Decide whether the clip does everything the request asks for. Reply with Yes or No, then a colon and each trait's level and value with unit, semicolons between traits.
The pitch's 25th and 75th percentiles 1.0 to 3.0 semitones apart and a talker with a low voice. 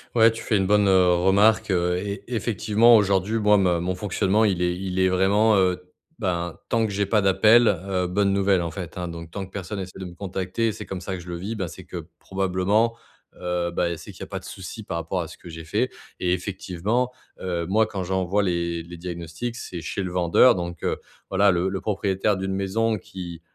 Yes: narrow, 2.6 semitones; very low, 95 Hz